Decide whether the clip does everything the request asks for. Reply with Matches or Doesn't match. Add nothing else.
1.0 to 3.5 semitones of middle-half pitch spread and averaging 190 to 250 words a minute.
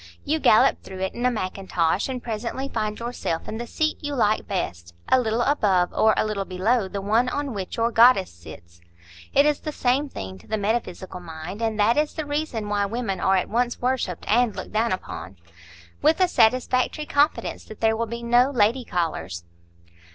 Doesn't match